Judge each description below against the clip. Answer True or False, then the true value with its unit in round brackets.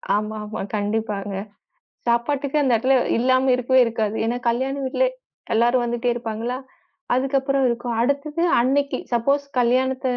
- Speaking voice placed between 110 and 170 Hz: False (245 Hz)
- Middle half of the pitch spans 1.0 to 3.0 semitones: True (2.5 semitones)